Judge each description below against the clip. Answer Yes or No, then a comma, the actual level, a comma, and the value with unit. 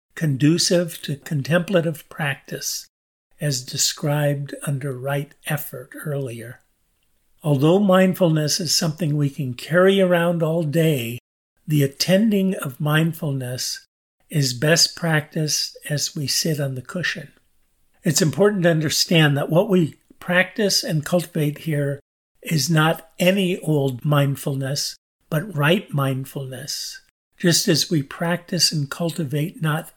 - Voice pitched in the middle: Yes, medium, 155 Hz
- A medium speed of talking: No, slow, 120 wpm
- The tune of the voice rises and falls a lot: No, average, 3.7 semitones